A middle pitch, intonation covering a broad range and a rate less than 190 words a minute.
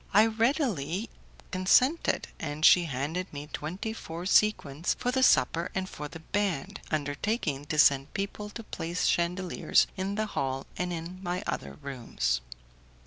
Yes: medium, 175 Hz; wide, 5.8 semitones; average, 145 wpm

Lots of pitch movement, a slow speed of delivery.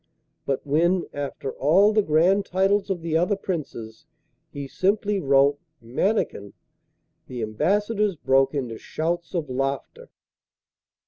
Yes: wide, 6.3 semitones; slow, 120 wpm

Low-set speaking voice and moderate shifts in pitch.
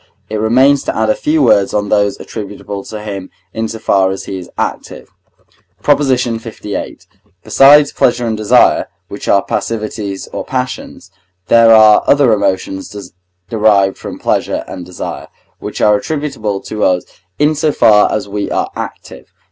Yes: low, 110 Hz; average, 3.5 semitones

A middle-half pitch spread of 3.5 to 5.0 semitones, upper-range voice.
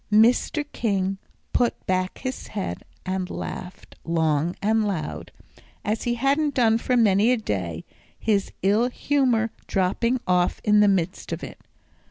Yes: average, 4.5 semitones; high, 210 Hz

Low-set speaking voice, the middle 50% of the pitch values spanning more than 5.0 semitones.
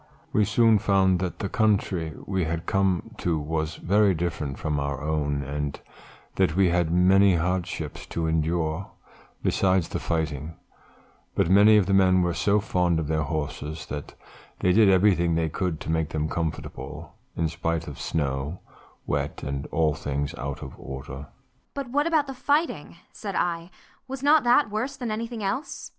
No: very low, 85 Hz; average, 4.7 semitones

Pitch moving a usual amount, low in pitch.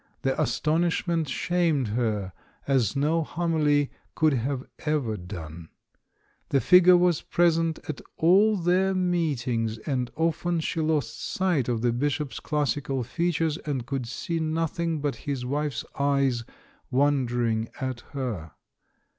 No: average, 5.0 semitones; medium, 145 Hz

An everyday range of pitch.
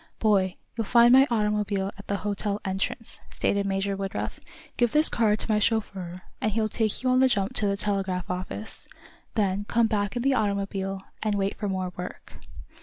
No: narrow, 2.2 semitones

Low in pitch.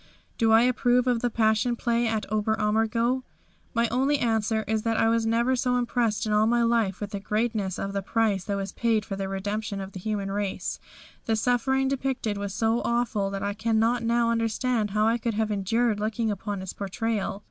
No: high, 225 Hz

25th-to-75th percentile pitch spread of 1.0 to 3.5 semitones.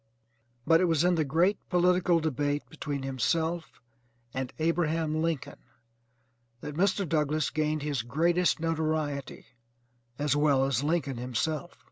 Yes: average, 2.7 semitones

